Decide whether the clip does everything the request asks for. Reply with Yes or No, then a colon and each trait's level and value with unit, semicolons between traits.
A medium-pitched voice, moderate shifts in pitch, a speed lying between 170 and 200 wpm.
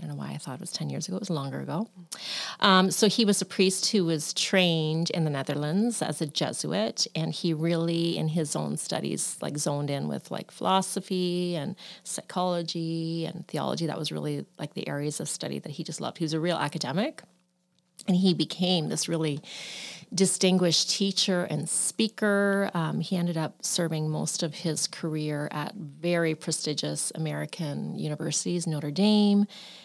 Yes: medium, 170 Hz; average, 3.3 semitones; average, 180 wpm